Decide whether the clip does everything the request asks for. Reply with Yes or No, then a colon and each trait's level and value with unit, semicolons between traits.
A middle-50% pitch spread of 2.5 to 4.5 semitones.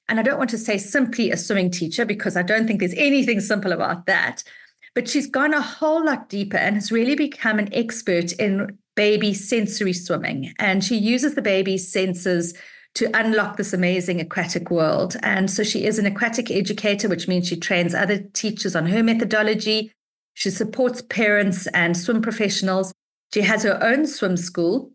Yes: average, 3.4 semitones